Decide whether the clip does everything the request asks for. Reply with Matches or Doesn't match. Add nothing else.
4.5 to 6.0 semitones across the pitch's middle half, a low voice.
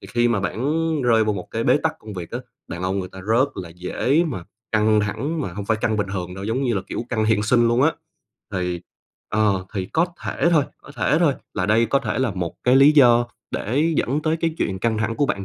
Matches